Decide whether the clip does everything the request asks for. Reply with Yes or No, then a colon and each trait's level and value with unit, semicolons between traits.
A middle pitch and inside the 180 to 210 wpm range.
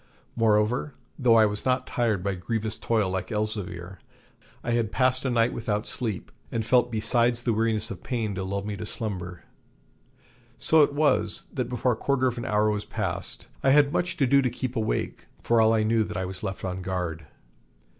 No: low, 110 Hz; average, 195 wpm